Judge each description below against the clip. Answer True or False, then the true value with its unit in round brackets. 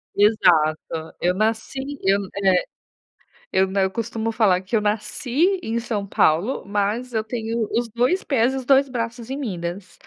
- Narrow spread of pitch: False (3.9 semitones)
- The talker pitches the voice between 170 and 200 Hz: False (220 Hz)